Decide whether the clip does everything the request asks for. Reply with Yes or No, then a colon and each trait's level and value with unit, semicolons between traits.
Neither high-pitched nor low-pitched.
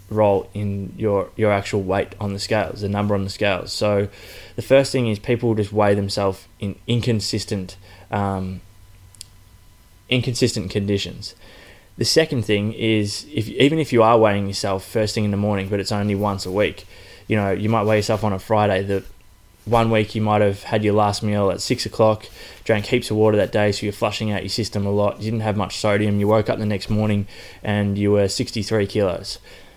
No: low, 105 Hz